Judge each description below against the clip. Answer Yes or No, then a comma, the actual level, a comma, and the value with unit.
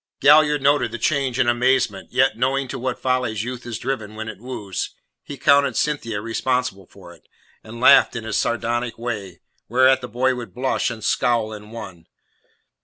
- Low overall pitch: Yes, low, 120 Hz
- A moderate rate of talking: Yes, average, 180 wpm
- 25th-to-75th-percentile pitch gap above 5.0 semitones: No, average, 2.9 semitones